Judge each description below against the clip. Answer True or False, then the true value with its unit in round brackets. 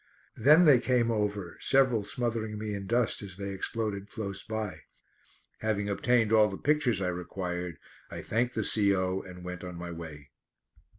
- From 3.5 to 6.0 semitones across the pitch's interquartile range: True (3.8 semitones)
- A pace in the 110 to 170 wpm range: True (165 wpm)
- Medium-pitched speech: False (105 Hz)